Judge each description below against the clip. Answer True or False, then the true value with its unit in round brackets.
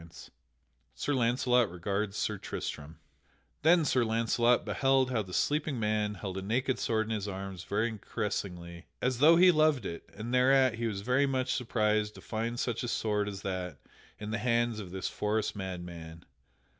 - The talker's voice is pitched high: False (110 Hz)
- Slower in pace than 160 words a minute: False (175 wpm)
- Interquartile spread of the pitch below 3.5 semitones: False (4.4 semitones)